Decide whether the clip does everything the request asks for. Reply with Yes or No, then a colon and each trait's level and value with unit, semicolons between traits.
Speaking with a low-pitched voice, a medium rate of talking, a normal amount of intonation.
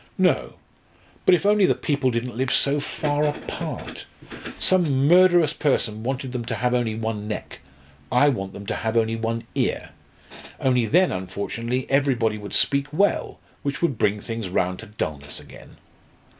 Yes: low, 125 Hz; average, 160 wpm; average, 4.6 semitones